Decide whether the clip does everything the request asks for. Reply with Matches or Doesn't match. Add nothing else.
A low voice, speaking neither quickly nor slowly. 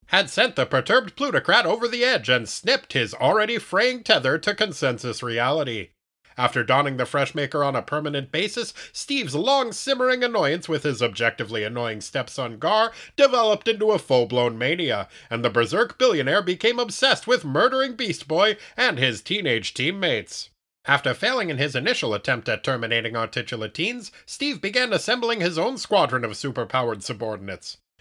Doesn't match